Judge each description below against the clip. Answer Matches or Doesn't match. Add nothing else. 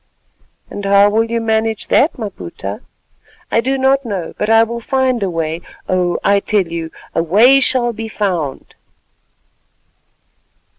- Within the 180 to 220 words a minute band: Doesn't match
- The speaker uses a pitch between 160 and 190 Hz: Doesn't match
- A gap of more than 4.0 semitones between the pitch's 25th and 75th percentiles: Matches